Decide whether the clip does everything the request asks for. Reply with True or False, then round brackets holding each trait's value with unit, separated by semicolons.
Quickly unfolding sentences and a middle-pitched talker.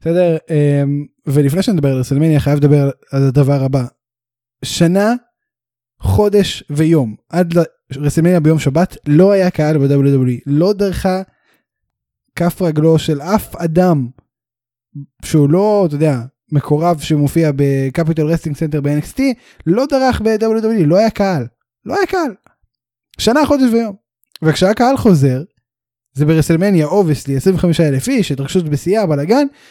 False (125 wpm; 160 Hz)